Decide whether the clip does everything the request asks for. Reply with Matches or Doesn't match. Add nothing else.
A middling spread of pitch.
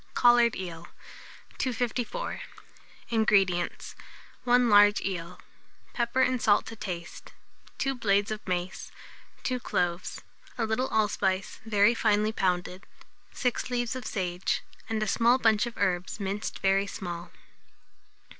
Matches